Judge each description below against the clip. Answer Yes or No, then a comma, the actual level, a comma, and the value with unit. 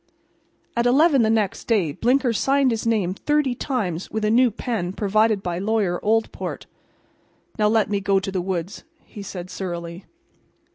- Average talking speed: Yes, average, 160 wpm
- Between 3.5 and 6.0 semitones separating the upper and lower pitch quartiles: Yes, average, 4.0 semitones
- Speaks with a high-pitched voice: Yes, high, 210 Hz